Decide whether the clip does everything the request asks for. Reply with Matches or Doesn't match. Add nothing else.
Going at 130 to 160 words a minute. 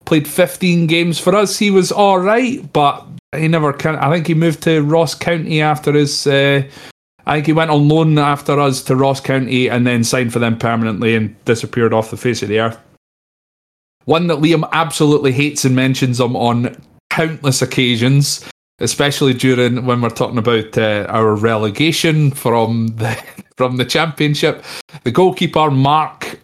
Doesn't match